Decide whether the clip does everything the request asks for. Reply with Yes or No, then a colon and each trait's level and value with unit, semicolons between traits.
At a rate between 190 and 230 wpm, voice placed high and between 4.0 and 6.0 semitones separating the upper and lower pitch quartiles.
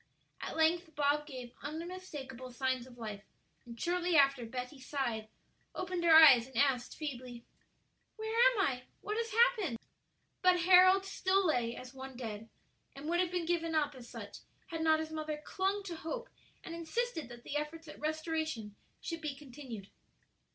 No: average, 165 wpm; very high, 305 Hz; average, 5.3 semitones